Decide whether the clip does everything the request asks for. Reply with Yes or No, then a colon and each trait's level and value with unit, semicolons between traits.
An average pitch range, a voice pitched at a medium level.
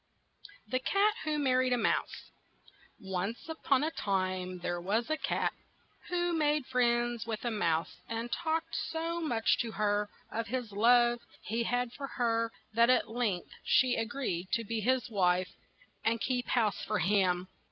No: average, 3.8 semitones; high, 235 Hz